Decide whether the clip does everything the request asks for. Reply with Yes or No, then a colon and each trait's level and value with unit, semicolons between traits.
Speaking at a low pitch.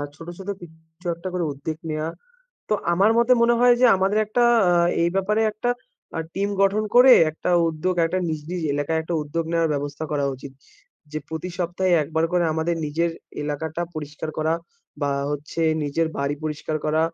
No: medium, 165 Hz